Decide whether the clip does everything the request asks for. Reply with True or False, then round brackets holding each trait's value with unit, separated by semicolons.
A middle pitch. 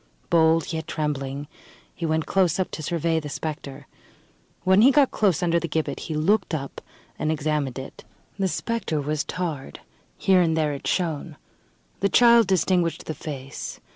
True (160 Hz)